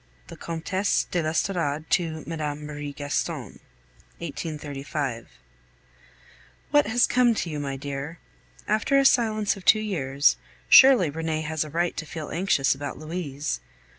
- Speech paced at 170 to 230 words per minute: No, average, 140 wpm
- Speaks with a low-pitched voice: No, medium, 160 Hz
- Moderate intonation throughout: Yes, average, 4.6 semitones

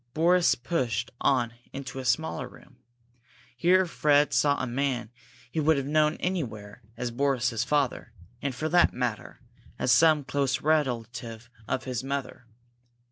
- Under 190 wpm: Yes, average, 140 wpm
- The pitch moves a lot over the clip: No, average, 4.0 semitones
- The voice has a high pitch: No, low, 135 Hz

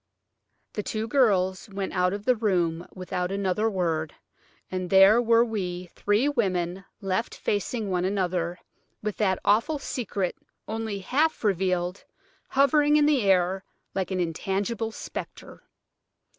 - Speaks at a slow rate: Yes, slow, 130 wpm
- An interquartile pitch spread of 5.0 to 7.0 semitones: No, average, 3.5 semitones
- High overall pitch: Yes, high, 195 Hz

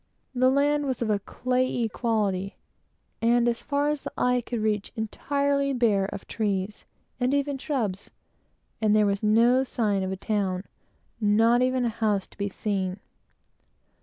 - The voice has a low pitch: No, high, 230 Hz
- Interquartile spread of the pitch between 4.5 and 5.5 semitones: No, average, 3.9 semitones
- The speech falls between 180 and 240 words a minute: No, average, 160 wpm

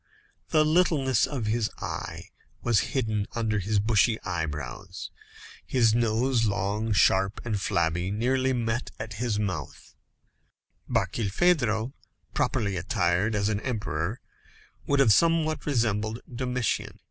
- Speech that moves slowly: Yes, slow, 110 wpm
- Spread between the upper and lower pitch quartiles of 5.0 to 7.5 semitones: No, average, 3.7 semitones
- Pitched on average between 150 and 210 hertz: No, low, 110 Hz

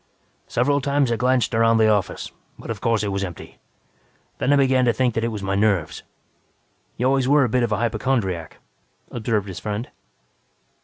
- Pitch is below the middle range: Yes, low, 115 Hz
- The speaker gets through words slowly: No, average, 190 wpm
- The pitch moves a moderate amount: Yes, average, 3.7 semitones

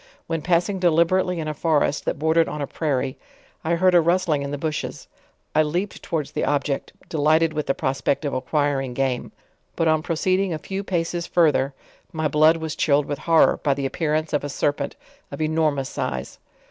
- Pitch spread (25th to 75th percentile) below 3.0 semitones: Yes, narrow, 2.5 semitones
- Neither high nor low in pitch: Yes, medium, 155 Hz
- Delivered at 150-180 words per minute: No, average, 190 wpm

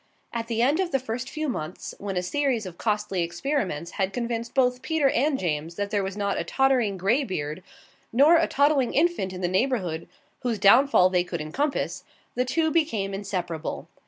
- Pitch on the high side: Yes, high, 225 Hz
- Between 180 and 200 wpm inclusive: Yes, average, 190 wpm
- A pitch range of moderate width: No, wide, 6.6 semitones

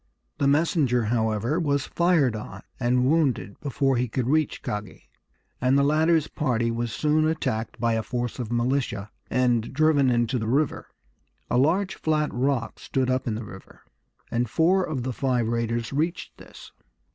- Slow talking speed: No, average, 165 wpm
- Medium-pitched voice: No, low, 130 Hz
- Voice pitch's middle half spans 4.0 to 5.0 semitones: Yes, average, 4.4 semitones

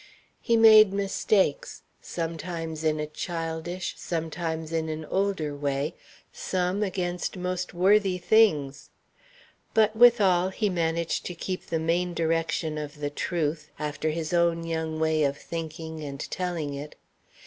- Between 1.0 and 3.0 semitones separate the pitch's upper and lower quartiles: Yes, narrow, 2.6 semitones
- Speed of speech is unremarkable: No, slow, 130 wpm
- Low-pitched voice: No, medium, 165 Hz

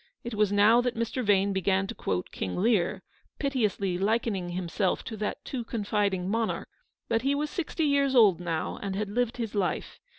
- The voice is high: Yes, high, 210 Hz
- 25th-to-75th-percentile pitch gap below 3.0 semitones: No, average, 3.7 semitones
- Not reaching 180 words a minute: No, average, 190 wpm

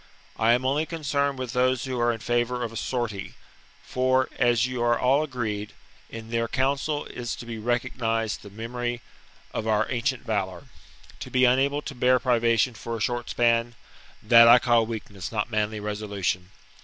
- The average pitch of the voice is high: No, low, 120 Hz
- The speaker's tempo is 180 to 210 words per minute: Yes, average, 190 wpm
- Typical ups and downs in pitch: No, narrow, 2.3 semitones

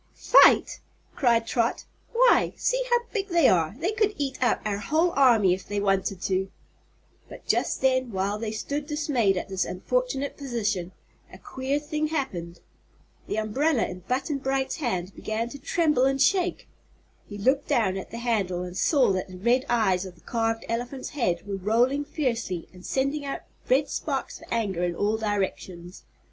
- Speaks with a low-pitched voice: No, high, 235 Hz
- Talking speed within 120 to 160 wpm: No, average, 175 wpm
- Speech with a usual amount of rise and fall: No, wide, 6.5 semitones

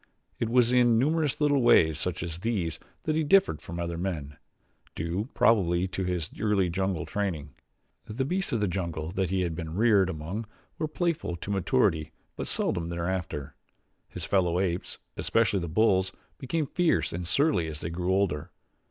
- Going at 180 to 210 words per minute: No, average, 170 wpm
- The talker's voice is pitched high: No, very low, 95 Hz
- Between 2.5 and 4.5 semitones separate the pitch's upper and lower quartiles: No, wide, 5.4 semitones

